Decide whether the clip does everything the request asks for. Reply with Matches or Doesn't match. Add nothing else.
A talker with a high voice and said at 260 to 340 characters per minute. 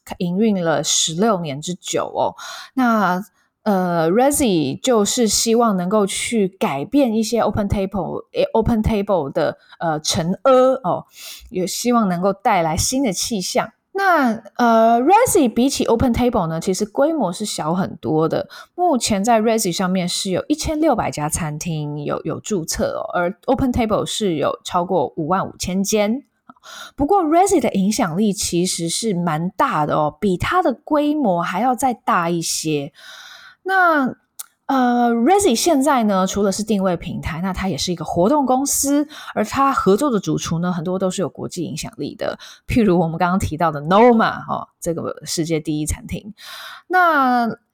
Matches